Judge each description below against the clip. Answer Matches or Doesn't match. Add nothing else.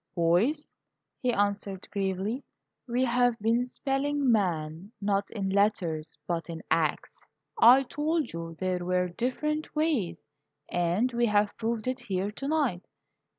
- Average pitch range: Doesn't match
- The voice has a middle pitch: Doesn't match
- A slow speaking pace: Matches